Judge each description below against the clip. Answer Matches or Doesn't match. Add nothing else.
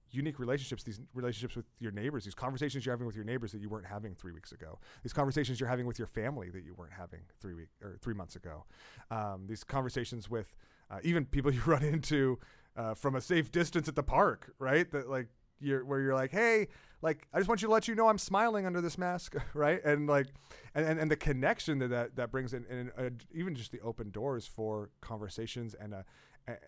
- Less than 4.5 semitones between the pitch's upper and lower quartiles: Doesn't match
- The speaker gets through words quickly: Matches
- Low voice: Matches